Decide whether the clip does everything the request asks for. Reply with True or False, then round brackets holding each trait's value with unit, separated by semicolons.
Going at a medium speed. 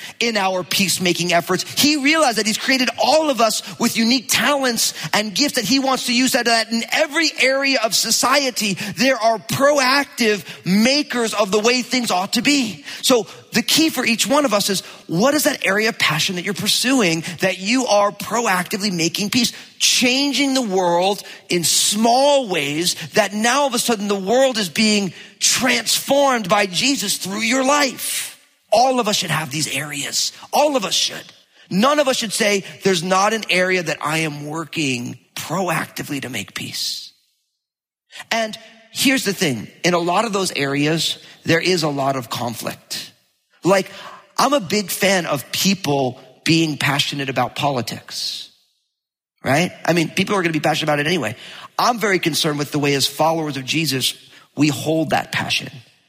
True (180 wpm)